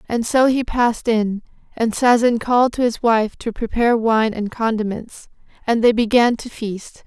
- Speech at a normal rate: Yes, average, 180 wpm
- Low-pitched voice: No, high, 230 Hz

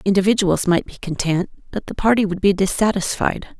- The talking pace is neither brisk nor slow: Yes, average, 165 wpm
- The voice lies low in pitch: No, high, 190 Hz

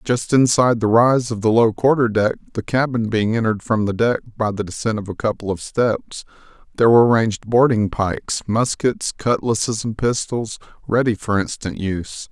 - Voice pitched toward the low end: Yes, low, 110 Hz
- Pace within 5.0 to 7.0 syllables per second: Yes, 5.2 syllables/s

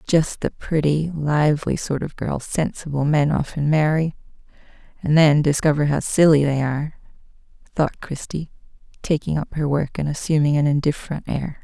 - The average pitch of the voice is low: No, medium, 150 Hz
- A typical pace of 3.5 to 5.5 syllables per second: Yes, 5.0 syllables/s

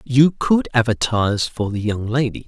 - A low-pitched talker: Yes, low, 120 Hz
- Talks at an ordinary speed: Yes, average, 170 wpm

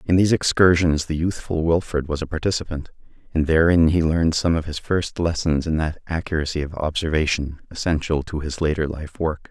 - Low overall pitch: Yes, very low, 80 Hz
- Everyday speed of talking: Yes, average, 185 wpm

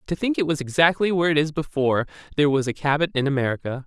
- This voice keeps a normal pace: No, fast, 235 wpm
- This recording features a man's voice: Yes, male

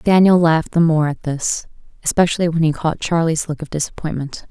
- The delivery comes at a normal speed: Yes, average, 185 wpm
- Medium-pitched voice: Yes, medium, 160 Hz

